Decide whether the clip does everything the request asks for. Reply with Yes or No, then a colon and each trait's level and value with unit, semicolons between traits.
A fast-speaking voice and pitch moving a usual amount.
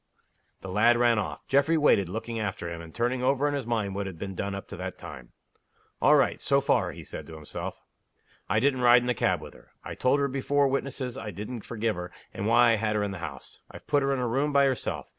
Yes: fast, 255 wpm; average, 5.0 semitones